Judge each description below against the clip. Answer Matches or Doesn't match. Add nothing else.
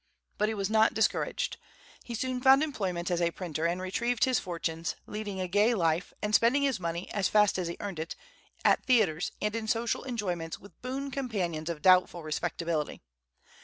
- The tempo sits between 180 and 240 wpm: Matches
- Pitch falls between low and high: Doesn't match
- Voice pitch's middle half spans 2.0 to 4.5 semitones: Doesn't match